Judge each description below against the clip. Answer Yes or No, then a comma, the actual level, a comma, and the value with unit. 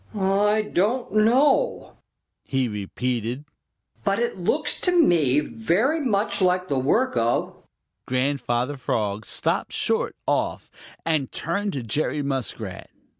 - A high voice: No, medium, 150 Hz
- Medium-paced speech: No, slow, 125 wpm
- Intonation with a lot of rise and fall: Yes, wide, 8.7 semitones